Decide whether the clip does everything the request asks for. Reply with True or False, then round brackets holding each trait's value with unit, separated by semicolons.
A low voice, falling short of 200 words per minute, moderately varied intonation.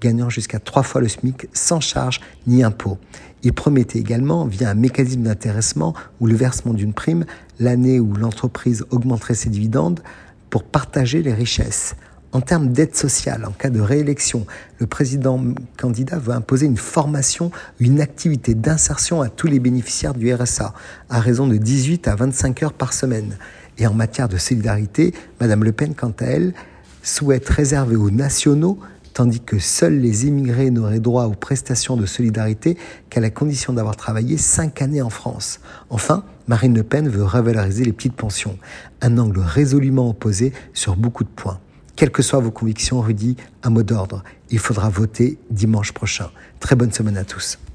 True (120 Hz; 170 wpm; 3.6 semitones)